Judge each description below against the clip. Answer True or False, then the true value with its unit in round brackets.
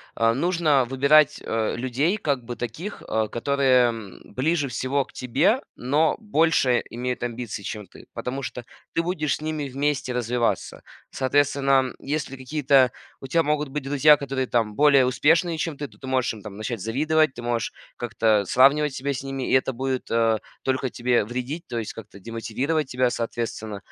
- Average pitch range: True (3.6 semitones)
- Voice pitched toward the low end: True (130 Hz)